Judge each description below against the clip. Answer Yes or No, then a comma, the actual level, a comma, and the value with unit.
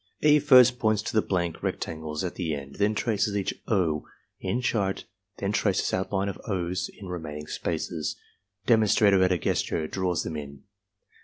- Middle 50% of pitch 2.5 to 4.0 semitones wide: No, average, 4.7 semitones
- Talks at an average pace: Yes, average, 165 wpm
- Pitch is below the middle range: Yes, very low, 95 Hz